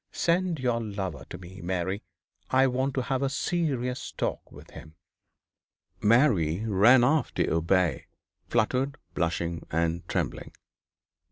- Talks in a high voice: No, low, 115 Hz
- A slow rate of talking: Yes, slow, 125 wpm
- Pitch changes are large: Yes, wide, 7.2 semitones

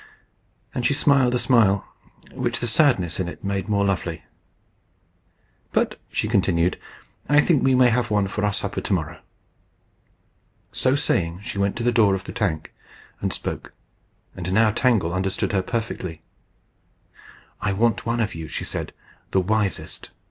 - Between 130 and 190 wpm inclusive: Yes, average, 155 wpm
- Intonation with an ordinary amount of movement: Yes, average, 4.2 semitones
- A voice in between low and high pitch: No, low, 105 Hz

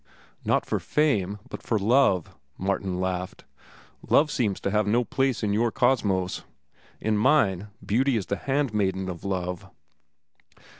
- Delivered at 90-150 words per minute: Yes, average, 140 wpm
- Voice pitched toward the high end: No, low, 105 Hz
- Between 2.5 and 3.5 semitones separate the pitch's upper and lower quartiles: No, average, 4.4 semitones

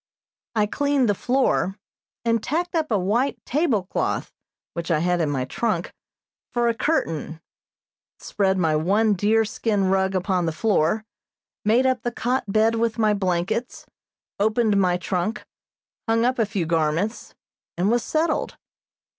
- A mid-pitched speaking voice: No, high, 210 Hz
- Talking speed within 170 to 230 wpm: No, average, 145 wpm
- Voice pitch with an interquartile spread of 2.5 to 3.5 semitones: No, average, 4.6 semitones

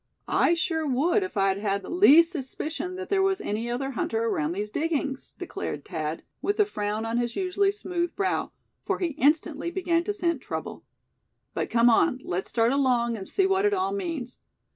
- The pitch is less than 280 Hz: No, very high, 300 Hz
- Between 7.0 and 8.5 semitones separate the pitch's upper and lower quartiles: Yes, wide, 7.9 semitones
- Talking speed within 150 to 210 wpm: Yes, average, 190 wpm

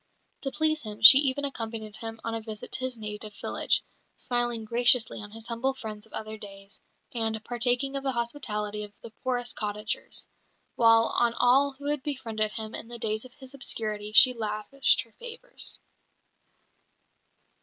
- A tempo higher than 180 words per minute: No, average, 165 wpm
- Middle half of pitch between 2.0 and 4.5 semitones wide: Yes, average, 3.2 semitones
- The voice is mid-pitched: No, high, 230 Hz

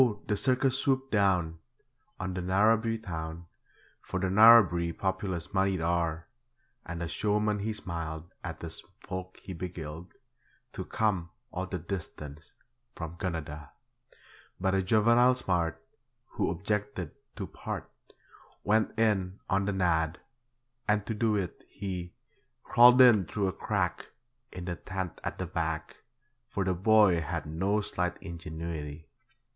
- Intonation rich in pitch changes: No, average, 3.8 semitones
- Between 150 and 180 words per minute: No, slow, 135 wpm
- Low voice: Yes, very low, 95 Hz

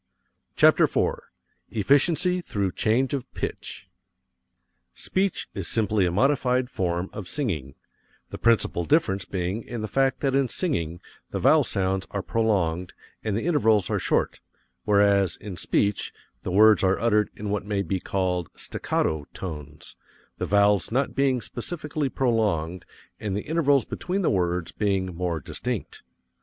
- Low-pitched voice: Yes, low, 105 Hz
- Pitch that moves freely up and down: Yes, wide, 5.7 semitones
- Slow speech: No, average, 145 wpm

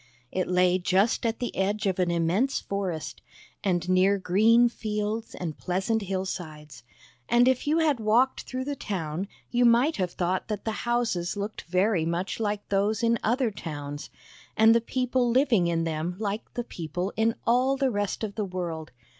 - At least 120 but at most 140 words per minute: No, average, 175 wpm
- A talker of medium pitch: No, high, 205 Hz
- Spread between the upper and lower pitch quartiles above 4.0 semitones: Yes, average, 4.6 semitones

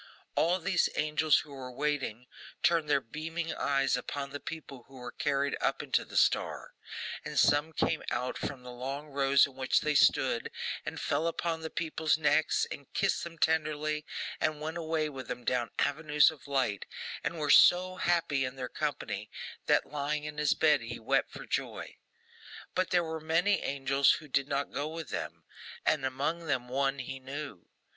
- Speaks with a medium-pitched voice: Yes, medium, 145 Hz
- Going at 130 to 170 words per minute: No, average, 180 wpm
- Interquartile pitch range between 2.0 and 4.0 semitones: Yes, average, 2.9 semitones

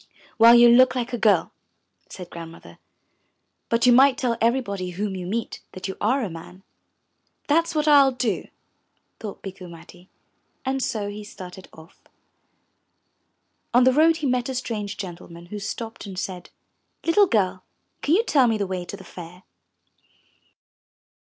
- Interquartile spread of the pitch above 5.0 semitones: Yes, wide, 5.4 semitones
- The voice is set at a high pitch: Yes, high, 210 Hz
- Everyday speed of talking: Yes, average, 160 wpm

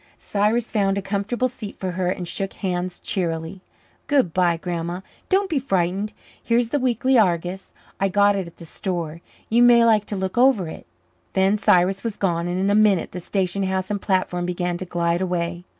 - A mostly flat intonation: No, average, 3.2 semitones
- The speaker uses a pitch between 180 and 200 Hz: Yes, high, 190 Hz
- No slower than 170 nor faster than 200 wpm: Yes, average, 195 wpm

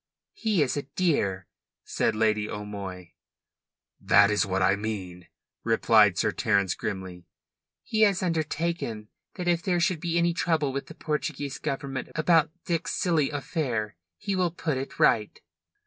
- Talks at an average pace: Yes, average, 150 wpm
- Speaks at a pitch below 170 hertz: Yes, medium, 140 Hz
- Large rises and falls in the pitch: Yes, wide, 8.5 semitones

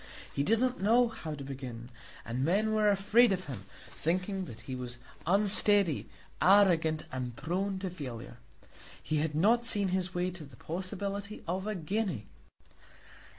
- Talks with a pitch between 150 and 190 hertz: Yes, medium, 185 Hz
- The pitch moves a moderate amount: No, wide, 5.8 semitones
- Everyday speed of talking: Yes, average, 155 wpm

